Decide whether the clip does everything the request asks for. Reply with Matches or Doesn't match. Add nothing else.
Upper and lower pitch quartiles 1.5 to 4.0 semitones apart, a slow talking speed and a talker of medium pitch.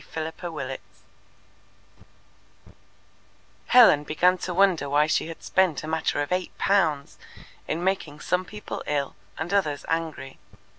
Matches